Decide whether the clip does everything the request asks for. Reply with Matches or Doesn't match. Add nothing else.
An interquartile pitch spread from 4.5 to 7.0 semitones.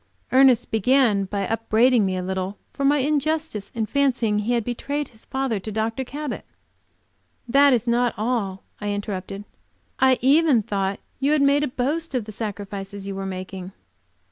Matches